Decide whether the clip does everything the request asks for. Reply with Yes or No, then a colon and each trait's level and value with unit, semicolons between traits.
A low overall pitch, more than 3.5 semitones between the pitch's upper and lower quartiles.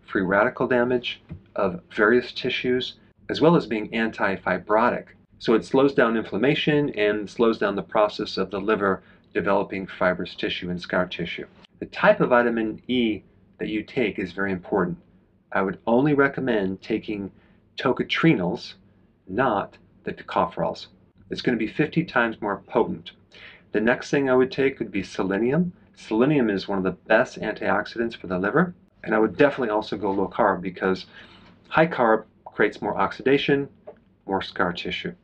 Yes: low, 115 Hz; average, 4.6 semitones